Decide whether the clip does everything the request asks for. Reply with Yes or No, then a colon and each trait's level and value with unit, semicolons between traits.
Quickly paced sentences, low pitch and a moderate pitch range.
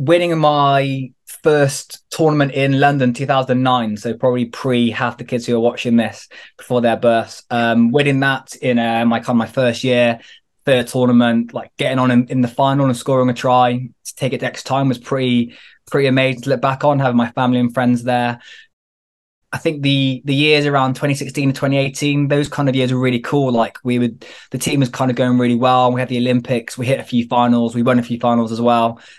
No: fast, 220 wpm; low, 125 Hz; narrow, 2.2 semitones